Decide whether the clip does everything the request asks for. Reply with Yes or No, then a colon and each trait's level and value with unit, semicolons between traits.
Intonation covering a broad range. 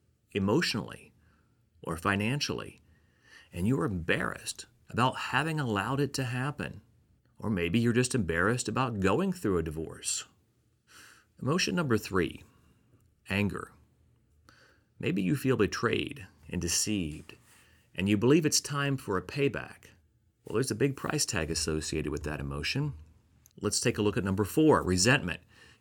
Yes: wide, 7.6 semitones